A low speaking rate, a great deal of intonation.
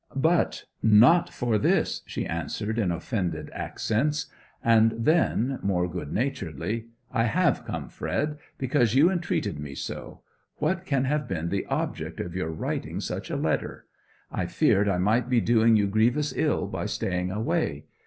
No: average, 155 wpm; wide, 6.1 semitones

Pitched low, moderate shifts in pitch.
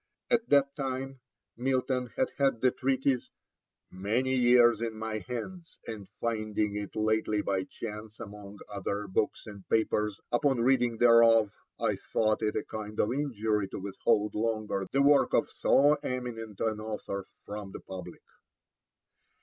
Yes: low, 110 Hz; average, 3.4 semitones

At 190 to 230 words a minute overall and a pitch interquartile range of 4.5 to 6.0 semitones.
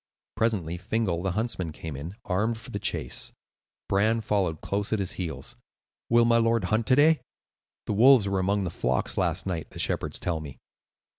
No: average, 180 wpm; average, 4.8 semitones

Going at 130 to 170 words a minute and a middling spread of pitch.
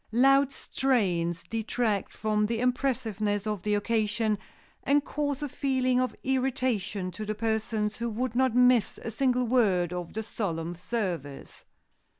Yes: average, 145 wpm; average, 3.6 semitones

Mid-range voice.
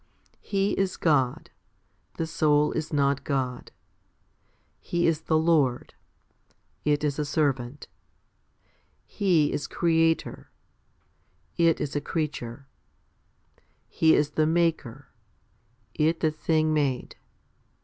Yes: medium, 150 Hz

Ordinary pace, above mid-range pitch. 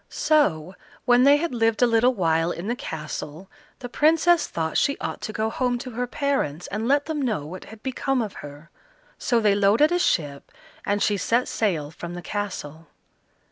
Yes: average, 190 wpm; high, 220 Hz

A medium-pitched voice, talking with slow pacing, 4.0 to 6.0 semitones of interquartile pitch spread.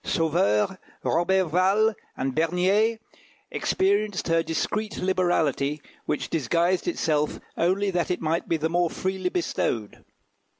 No: medium, 175 Hz; slow, 115 wpm; average, 2.9 semitones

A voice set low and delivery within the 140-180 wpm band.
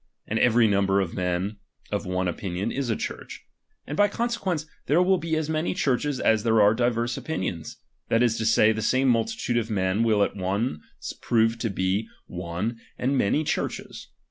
No: low, 115 Hz; average, 190 wpm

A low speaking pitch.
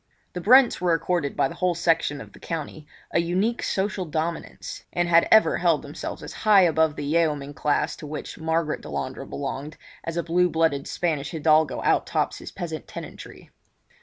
No: medium, 165 Hz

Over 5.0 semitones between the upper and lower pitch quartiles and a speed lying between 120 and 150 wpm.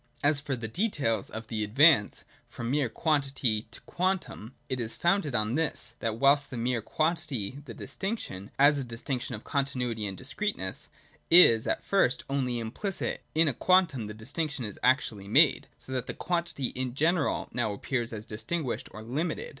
No: wide, 5.4 semitones; average, 170 wpm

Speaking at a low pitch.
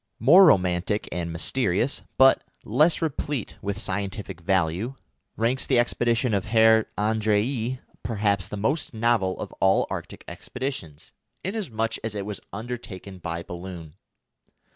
Yes: low, 105 Hz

